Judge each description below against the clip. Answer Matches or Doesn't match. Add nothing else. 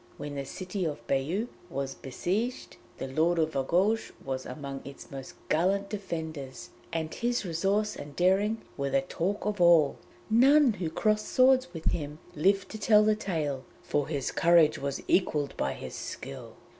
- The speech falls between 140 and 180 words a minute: Matches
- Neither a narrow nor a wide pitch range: Doesn't match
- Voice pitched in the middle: Matches